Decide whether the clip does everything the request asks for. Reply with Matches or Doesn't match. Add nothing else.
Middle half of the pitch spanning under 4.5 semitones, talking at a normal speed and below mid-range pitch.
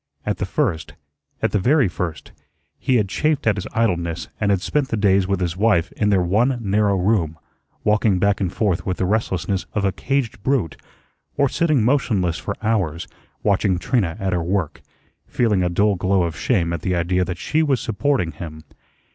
Matches